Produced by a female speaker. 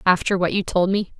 Yes: female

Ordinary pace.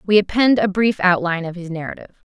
No: fast, 210 wpm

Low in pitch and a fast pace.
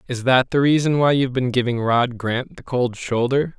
Yes: low, 125 Hz; fast, 220 wpm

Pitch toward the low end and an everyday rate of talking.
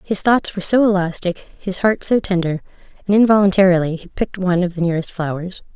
No: medium, 185 Hz; average, 190 wpm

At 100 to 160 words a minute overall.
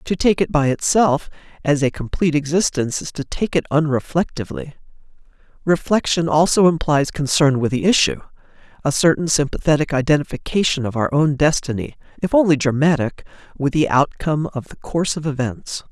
Yes: average, 145 wpm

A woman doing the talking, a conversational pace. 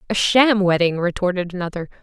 Yes: female; average, 150 wpm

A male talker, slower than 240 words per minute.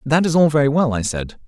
No: male; fast, 285 wpm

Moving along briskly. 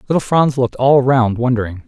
No: average, 190 wpm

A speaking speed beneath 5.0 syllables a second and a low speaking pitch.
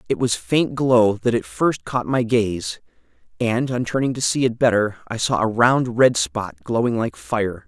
Yes: 4.3 syllables/s; low, 120 Hz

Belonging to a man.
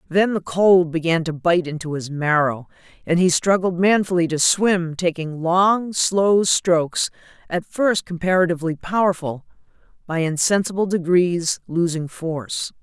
No: female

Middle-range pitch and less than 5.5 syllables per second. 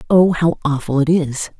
Yes: medium, 155 Hz; 4.7 syllables/s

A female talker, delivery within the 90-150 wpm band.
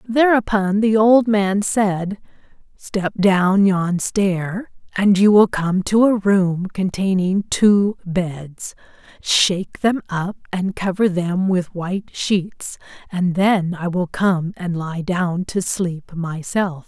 Yes: female; average, 140 wpm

